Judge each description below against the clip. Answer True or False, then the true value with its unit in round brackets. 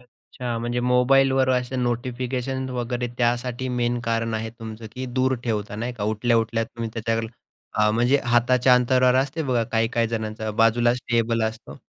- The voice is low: True (120 Hz)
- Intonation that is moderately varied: False (1.8 semitones)